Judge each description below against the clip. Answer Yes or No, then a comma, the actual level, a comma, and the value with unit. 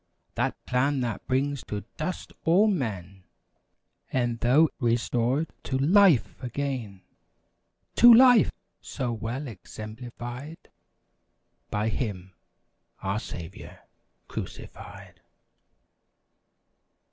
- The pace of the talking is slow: Yes, slow, 80 wpm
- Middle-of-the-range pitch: No, low, 125 Hz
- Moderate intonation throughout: Yes, average, 4.8 semitones